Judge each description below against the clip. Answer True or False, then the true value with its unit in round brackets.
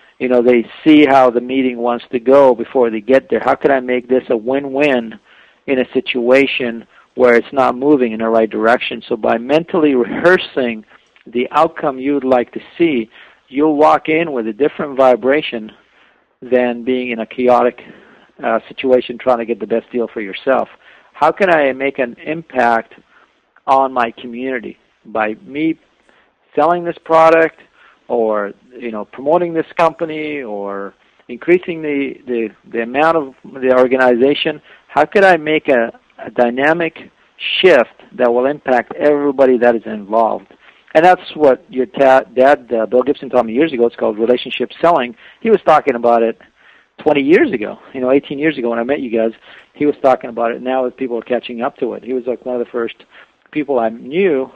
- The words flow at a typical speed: True (185 wpm)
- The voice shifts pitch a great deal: False (3.6 semitones)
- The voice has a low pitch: True (130 Hz)